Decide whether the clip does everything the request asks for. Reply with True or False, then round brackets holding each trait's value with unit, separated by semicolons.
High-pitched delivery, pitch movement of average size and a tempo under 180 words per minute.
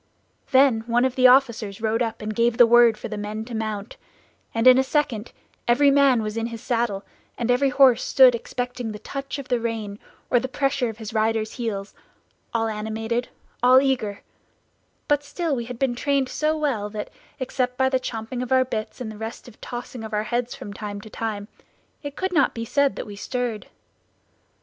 False (240 Hz; 3.0 semitones; 200 wpm)